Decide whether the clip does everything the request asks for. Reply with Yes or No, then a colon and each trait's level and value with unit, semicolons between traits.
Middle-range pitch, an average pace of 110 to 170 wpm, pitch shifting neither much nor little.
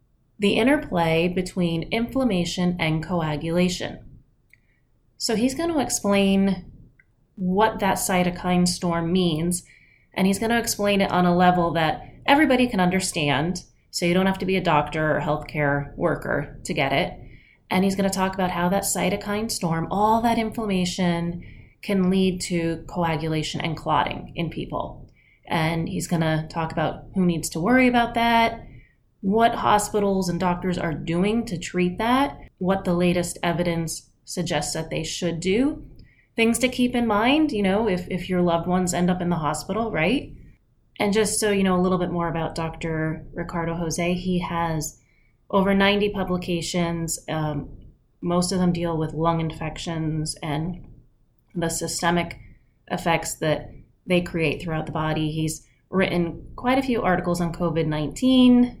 Yes: medium, 175 Hz; average, 160 wpm; average, 3.4 semitones